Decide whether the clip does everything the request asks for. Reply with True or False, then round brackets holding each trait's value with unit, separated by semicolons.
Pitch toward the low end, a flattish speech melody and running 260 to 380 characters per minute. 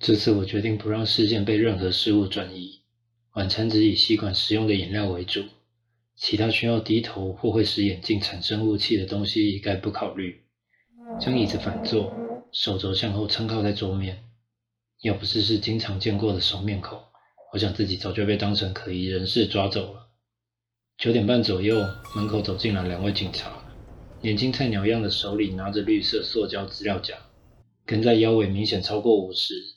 True (105 Hz; 2.3 semitones; 270 characters per minute)